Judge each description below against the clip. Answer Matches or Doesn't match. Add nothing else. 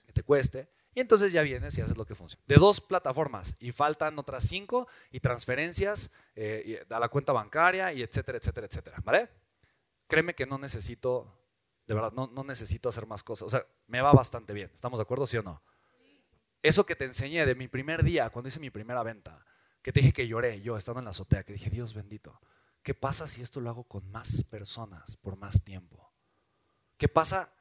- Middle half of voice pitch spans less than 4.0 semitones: Doesn't match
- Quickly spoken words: Matches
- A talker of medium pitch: Doesn't match